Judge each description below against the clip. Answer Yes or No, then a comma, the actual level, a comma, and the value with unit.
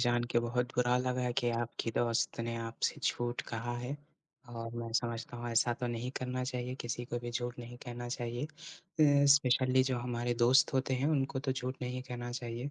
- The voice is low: Yes, low, 120 Hz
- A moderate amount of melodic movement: No, narrow, 1.3 semitones